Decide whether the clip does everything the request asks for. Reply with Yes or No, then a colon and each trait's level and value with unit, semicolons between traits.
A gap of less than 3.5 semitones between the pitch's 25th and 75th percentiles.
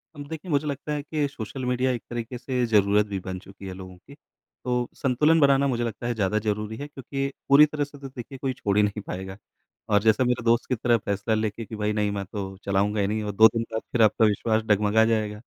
No: average, 4.0 semitones